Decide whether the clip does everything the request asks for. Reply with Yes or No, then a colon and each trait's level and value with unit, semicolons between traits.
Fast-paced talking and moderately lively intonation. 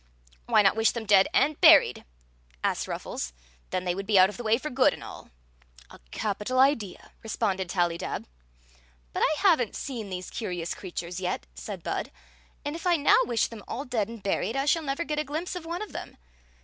No: fast, 215 wpm; wide, 7.5 semitones